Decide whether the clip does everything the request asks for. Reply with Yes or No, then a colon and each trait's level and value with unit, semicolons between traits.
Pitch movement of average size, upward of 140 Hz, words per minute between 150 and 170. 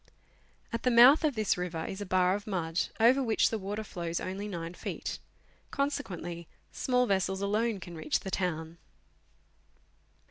Yes: average, 4.6 semitones; high, 190 Hz; average, 165 wpm